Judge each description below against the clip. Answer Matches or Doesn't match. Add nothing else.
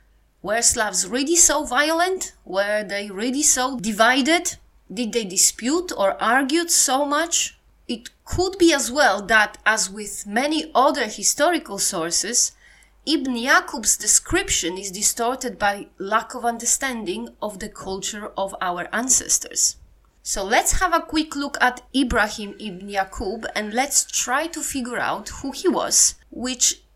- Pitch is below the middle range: Doesn't match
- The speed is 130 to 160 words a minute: Matches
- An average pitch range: Doesn't match